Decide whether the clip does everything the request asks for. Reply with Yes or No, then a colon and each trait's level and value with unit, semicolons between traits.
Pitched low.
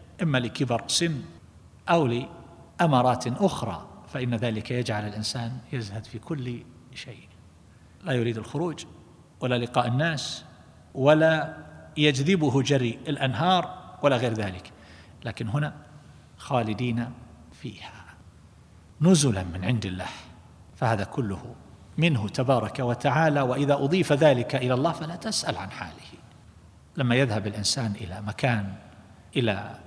Yes: low, 125 Hz